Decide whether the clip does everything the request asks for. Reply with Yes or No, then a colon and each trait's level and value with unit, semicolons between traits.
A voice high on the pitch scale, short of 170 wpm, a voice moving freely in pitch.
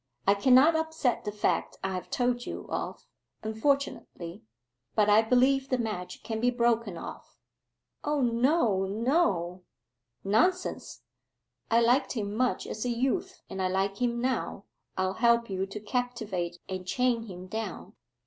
No: high, 230 Hz; average, 150 wpm; average, 4.3 semitones